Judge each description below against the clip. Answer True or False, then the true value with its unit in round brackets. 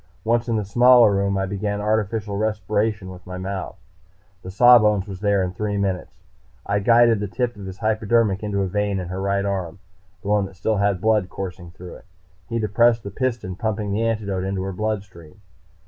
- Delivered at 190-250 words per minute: True (195 wpm)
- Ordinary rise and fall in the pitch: False (2.3 semitones)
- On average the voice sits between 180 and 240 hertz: False (100 Hz)